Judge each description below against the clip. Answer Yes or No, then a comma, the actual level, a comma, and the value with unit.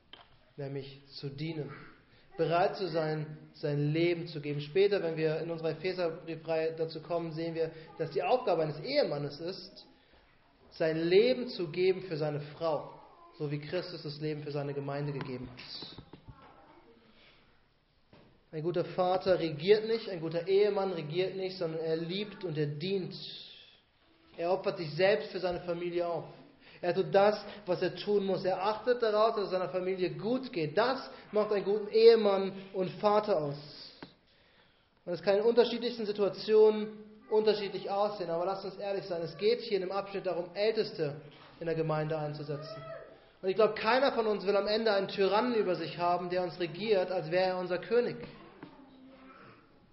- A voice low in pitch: No, medium, 180 Hz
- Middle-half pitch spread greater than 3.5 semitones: Yes, average, 4.0 semitones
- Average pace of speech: Yes, average, 165 wpm